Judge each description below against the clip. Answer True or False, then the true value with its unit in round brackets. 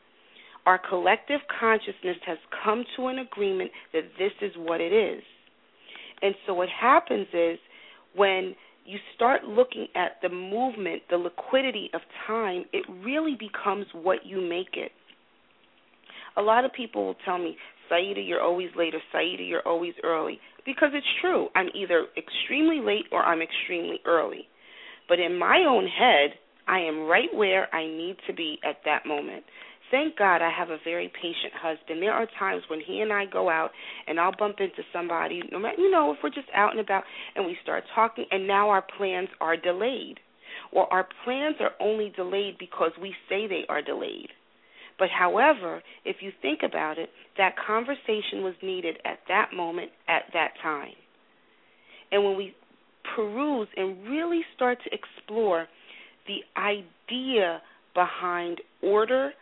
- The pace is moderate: True (165 wpm)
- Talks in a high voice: True (200 Hz)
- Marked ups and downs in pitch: True (6.5 semitones)